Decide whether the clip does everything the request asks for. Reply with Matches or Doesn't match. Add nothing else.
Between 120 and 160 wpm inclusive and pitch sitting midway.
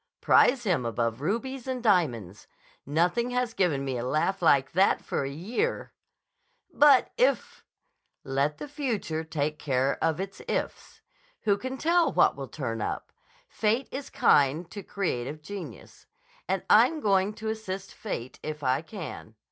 Matches